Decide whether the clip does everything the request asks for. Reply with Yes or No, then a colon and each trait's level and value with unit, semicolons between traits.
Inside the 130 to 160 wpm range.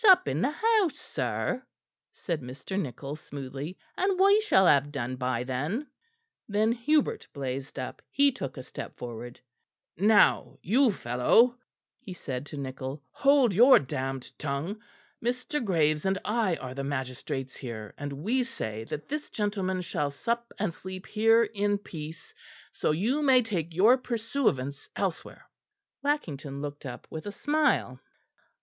Yes: average, 145 wpm